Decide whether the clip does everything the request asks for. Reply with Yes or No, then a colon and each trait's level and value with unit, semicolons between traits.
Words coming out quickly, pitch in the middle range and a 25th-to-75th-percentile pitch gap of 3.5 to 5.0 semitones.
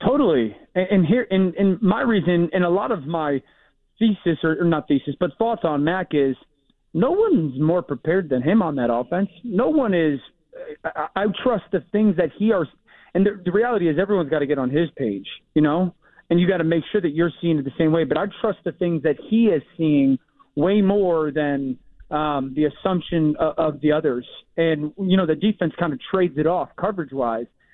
Yes: fast, 215 wpm; medium, 170 Hz; average, 4.4 semitones